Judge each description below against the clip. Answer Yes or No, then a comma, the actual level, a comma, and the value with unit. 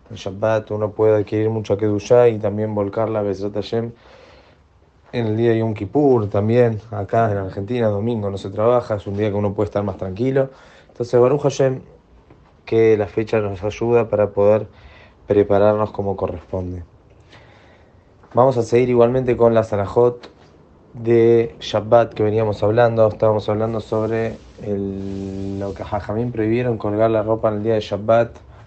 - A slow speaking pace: No, average, 155 wpm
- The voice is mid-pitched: No, low, 105 Hz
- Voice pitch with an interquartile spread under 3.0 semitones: Yes, narrow, 2.4 semitones